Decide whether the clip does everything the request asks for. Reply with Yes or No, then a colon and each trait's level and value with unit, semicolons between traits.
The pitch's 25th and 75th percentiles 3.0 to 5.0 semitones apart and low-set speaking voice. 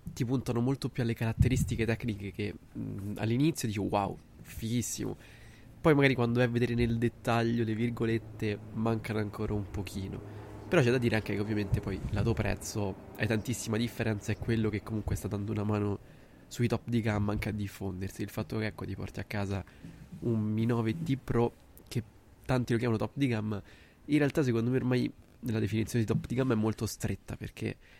No: narrow, 2.4 semitones; low, 110 Hz